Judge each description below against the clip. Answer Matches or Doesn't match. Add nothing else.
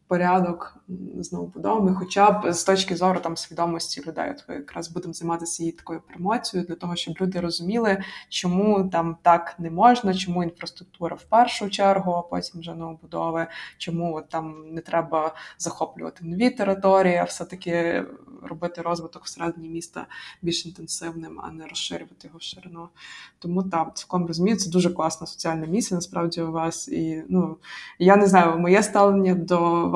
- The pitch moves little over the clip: Matches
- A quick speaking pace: Matches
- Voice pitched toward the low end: Doesn't match